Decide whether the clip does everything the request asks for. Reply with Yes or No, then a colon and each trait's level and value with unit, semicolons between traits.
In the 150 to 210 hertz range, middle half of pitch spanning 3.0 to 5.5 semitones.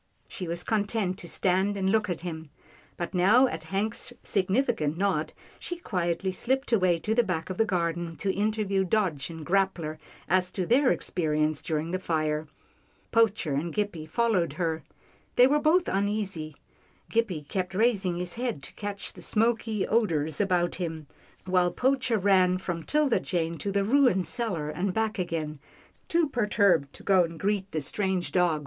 Yes: medium, 185 Hz; average, 4.4 semitones